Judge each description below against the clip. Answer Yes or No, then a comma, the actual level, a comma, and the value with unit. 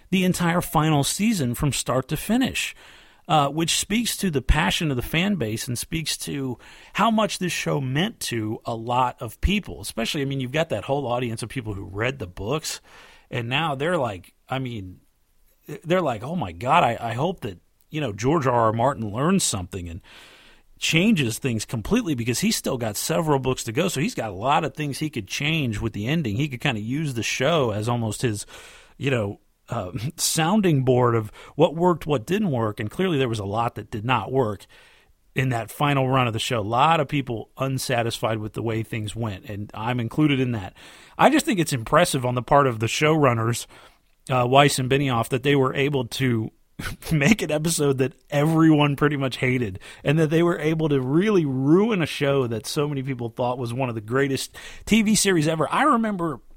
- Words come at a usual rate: No, fast, 210 wpm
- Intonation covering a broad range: No, average, 5.0 semitones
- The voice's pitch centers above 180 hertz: No, low, 135 Hz